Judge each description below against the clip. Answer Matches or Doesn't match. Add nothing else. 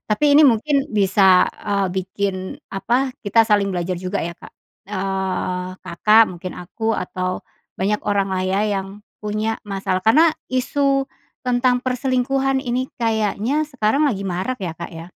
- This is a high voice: Matches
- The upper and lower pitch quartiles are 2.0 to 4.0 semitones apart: Doesn't match